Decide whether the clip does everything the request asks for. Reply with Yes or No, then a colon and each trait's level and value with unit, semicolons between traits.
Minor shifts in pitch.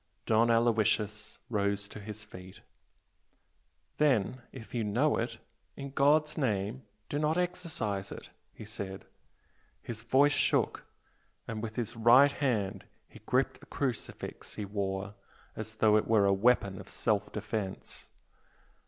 No: average, 4.0 semitones